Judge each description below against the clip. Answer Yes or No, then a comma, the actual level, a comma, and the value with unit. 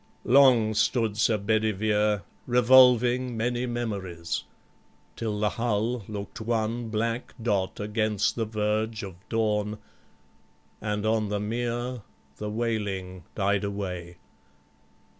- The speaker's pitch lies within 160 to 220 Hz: No, low, 110 Hz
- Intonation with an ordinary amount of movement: No, narrow, 2.2 semitones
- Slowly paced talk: Yes, slow, 105 wpm